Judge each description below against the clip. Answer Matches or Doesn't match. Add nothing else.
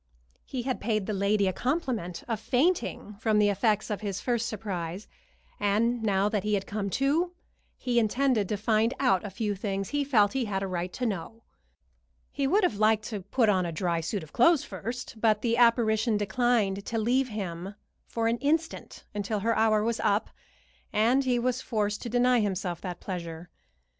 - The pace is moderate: Matches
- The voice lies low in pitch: Doesn't match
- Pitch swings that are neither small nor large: Matches